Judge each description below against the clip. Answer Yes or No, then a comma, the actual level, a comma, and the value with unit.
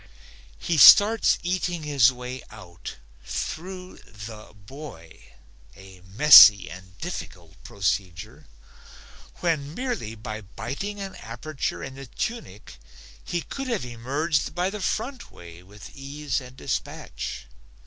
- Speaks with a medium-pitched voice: No, low, 130 Hz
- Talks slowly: Yes, slow, 120 wpm